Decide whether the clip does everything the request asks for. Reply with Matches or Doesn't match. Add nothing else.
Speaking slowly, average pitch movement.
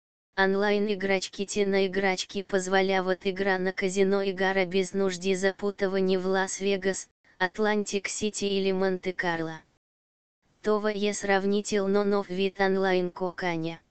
Doesn't match